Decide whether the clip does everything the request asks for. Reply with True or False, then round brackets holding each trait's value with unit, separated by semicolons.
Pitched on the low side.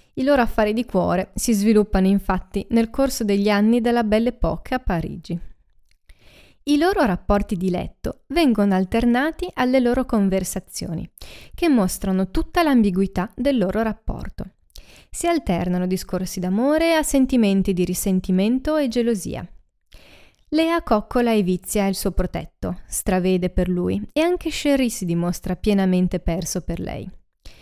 False (205 Hz)